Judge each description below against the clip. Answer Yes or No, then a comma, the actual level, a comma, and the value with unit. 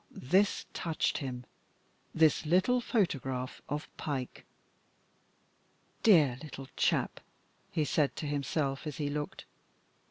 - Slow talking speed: Yes, slow, 105 wpm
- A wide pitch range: No, average, 3.1 semitones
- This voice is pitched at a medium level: Yes, medium, 150 Hz